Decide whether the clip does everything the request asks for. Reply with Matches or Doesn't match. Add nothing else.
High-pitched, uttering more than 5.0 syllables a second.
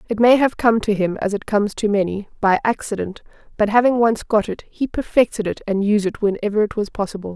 Matches